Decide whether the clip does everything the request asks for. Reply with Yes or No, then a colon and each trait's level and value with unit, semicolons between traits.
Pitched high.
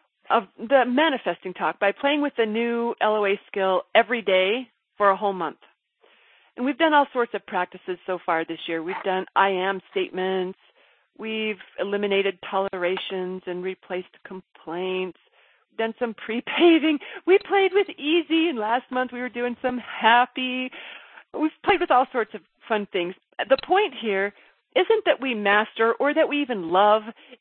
Yes: high, 225 Hz